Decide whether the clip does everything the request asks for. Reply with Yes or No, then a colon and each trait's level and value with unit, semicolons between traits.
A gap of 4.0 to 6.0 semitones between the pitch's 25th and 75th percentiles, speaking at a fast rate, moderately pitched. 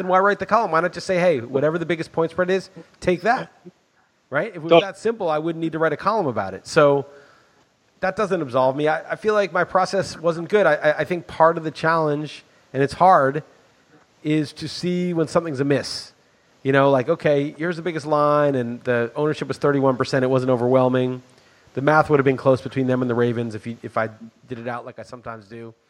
Yes: average, 4.9 semitones; fast, 230 wpm; medium, 150 Hz